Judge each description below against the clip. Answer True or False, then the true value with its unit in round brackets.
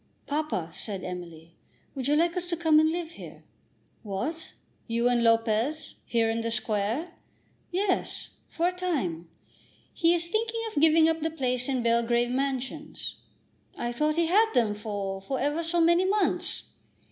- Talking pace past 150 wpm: True (160 wpm)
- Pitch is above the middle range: True (275 Hz)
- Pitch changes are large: True (6.6 semitones)